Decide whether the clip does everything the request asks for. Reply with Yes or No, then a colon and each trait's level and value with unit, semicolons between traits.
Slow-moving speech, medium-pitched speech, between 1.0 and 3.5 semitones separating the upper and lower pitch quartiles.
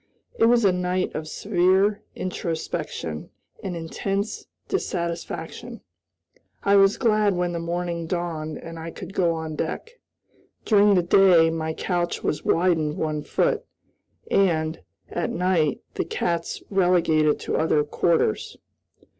Yes: slow, 130 wpm; medium, 175 Hz; average, 2.9 semitones